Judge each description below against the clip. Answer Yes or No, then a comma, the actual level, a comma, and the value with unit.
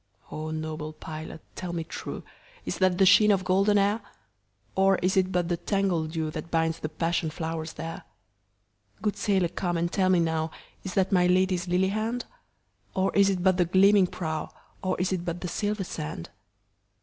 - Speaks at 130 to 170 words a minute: Yes, average, 160 wpm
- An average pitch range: Yes, average, 3.2 semitones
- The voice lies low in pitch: No, medium, 175 Hz